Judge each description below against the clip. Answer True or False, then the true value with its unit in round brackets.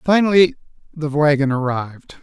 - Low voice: False (150 Hz)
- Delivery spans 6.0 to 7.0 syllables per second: False (5.1 syllables/s)